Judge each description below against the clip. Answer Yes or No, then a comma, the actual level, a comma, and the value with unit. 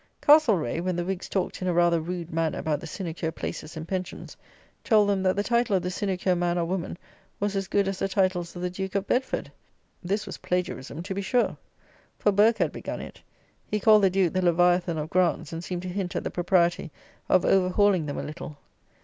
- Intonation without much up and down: Yes, narrow, 2.2 semitones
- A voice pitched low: No, medium, 185 Hz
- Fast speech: Yes, fast, 220 wpm